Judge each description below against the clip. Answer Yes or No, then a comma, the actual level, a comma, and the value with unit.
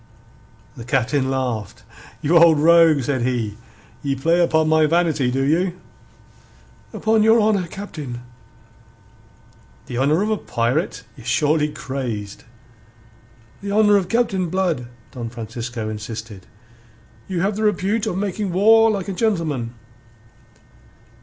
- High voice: No, medium, 160 Hz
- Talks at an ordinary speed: No, slow, 125 wpm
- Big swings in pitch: Yes, wide, 7.6 semitones